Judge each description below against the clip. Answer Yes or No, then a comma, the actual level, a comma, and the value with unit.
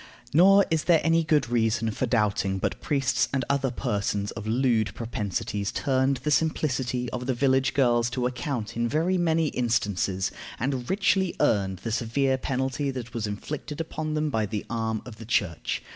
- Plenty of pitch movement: No, average, 4.3 semitones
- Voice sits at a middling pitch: No, low, 125 Hz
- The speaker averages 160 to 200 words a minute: Yes, average, 175 wpm